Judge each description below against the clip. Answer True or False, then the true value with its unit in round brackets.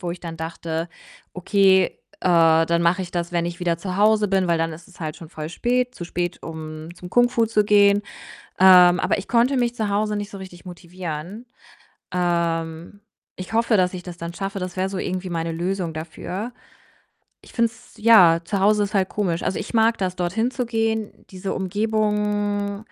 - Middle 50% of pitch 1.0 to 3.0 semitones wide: False (3.5 semitones)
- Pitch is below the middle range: False (185 Hz)